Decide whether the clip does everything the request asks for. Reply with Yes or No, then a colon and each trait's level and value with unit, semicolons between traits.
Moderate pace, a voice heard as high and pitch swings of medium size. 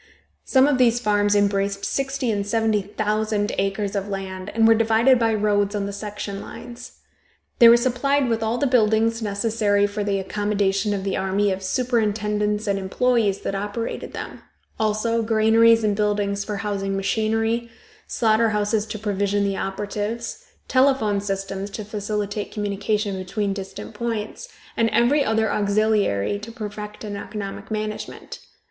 No: average, 150 wpm; high, 210 Hz; narrow, 1.9 semitones